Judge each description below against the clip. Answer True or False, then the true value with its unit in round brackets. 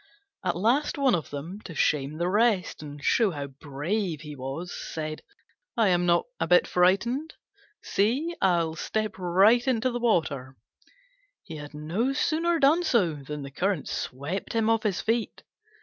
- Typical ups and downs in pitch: False (6.9 semitones)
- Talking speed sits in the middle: True (165 wpm)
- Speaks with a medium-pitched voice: True (180 Hz)